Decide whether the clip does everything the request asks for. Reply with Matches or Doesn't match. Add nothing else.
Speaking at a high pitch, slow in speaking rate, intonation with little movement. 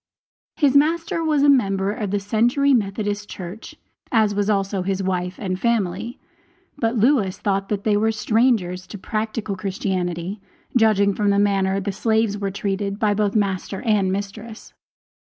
Doesn't match